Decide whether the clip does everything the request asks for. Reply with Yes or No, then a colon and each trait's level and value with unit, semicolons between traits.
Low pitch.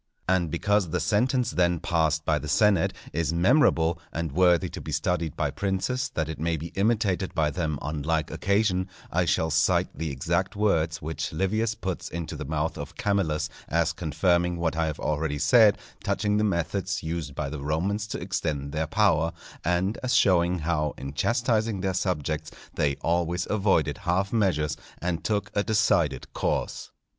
Yes: very low, 85 Hz